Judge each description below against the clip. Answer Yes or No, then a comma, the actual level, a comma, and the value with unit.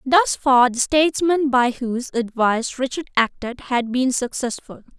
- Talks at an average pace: Yes, average, 145 wpm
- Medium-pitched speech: No, very high, 255 Hz